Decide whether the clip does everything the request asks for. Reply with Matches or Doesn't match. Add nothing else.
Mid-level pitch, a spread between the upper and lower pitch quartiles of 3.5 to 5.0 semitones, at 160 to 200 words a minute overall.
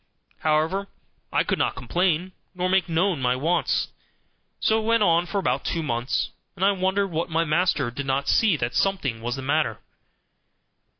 Doesn't match